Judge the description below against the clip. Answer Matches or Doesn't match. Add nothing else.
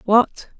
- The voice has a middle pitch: Doesn't match